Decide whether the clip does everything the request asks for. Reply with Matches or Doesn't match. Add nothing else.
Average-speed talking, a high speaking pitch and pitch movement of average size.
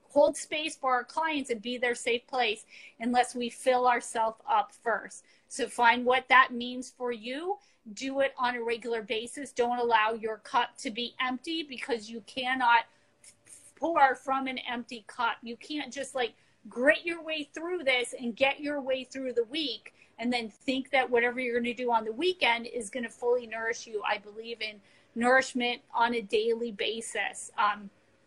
Doesn't match